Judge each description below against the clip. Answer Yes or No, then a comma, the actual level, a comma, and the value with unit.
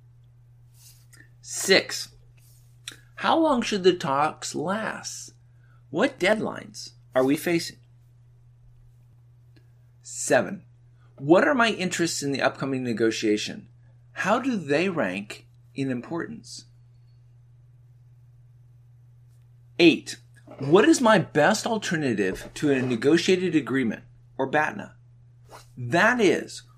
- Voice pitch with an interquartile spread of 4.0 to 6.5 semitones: No, average, 3.2 semitones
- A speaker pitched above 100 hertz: Yes, low, 120 Hz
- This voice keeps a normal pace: No, slow, 90 wpm